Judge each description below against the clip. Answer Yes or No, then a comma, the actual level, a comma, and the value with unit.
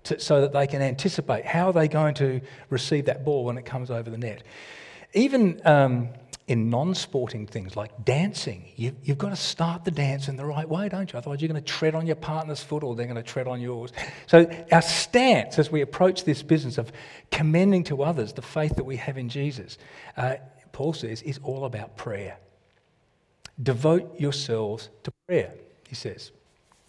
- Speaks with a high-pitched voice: No, medium, 140 Hz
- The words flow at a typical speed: Yes, average, 195 wpm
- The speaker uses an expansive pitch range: No, average, 4.5 semitones